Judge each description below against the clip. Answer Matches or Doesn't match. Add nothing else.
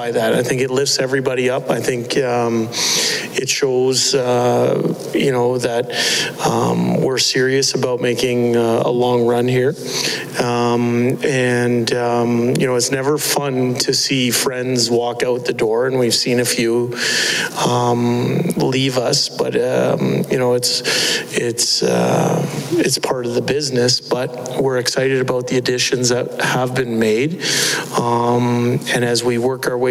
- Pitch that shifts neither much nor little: Doesn't match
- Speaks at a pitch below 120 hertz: Doesn't match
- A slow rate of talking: Doesn't match